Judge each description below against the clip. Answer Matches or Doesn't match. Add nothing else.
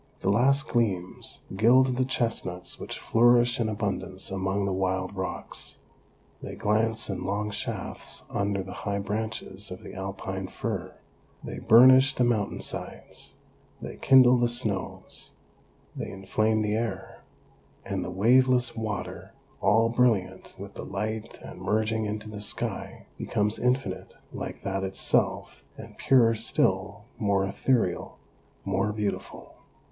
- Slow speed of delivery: Matches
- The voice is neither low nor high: Doesn't match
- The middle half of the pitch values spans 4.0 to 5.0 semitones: Doesn't match